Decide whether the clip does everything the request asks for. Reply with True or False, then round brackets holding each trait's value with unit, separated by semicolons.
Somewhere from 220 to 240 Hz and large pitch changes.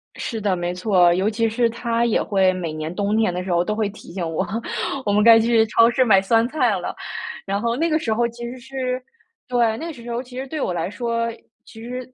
False (225 Hz; 3.7 semitones)